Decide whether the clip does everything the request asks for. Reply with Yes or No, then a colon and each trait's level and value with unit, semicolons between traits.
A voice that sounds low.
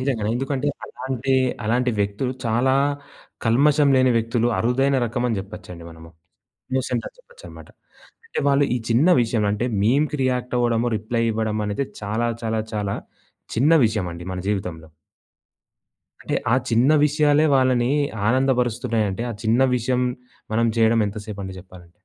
Yes: low, 120 Hz